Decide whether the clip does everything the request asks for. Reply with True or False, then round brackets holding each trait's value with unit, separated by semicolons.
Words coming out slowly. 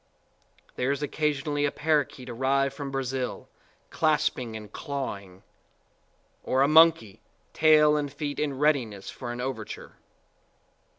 True (120 wpm)